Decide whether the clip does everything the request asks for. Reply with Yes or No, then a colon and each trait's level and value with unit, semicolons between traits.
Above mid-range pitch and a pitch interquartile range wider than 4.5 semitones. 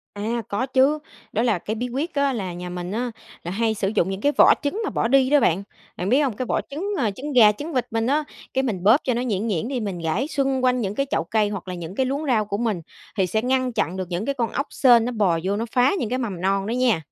Yes: high, 230 Hz; average, 4.9 semitones